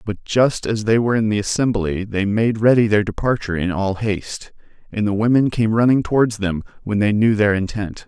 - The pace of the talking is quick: Yes, fast, 210 wpm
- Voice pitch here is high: No, low, 105 Hz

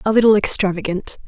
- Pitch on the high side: Yes, high, 200 Hz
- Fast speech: No, average, 140 wpm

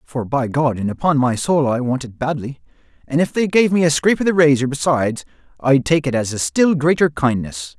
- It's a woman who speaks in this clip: No, male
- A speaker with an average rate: No, fast, 230 wpm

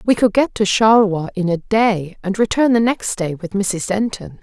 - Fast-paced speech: Yes, fast, 215 wpm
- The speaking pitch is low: No, high, 205 Hz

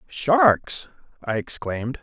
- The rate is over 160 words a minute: No, slow, 90 wpm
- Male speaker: Yes, male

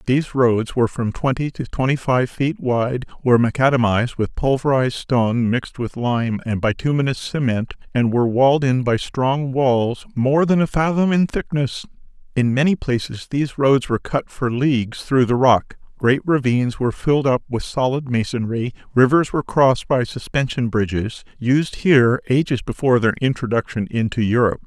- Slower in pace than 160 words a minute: No, average, 165 wpm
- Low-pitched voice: Yes, low, 130 Hz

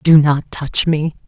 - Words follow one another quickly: No, average, 190 wpm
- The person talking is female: Yes, female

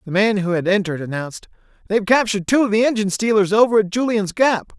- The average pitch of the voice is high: Yes, high, 205 Hz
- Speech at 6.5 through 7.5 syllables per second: Yes, 6.8 syllables/s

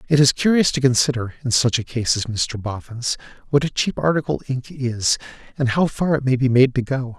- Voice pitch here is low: Yes, low, 130 Hz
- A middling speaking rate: No, fast, 225 wpm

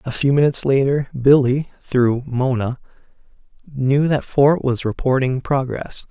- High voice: No, low, 135 Hz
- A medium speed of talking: No, slow, 130 wpm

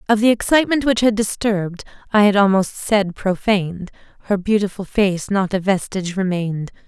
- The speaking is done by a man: No, female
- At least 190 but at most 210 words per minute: No, average, 140 wpm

